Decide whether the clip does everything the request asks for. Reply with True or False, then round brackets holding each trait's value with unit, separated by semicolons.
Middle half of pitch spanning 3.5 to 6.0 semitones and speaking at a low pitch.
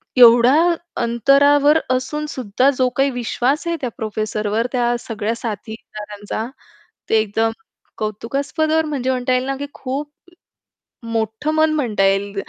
False (4.1 semitones; 245 Hz)